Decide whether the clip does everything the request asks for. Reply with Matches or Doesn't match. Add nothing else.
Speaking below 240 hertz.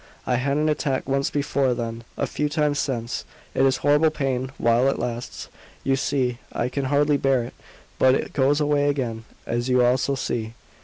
Matches